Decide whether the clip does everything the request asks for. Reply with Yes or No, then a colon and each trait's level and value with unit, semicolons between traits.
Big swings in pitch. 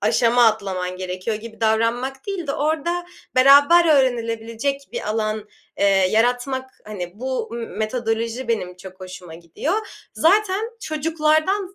Yes: wide, 5.9 semitones